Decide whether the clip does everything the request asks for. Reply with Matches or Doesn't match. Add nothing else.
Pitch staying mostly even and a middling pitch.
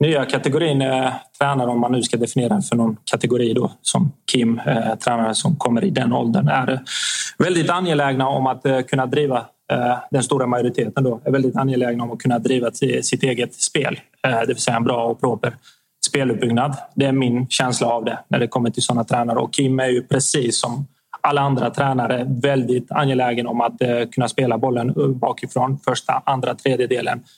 Doesn't match